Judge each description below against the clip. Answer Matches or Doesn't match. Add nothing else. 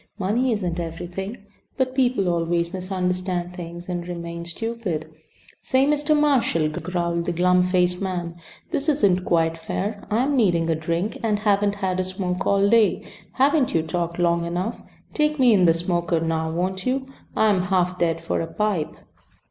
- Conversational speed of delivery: Matches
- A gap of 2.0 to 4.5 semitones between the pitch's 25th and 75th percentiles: Matches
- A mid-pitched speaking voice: Matches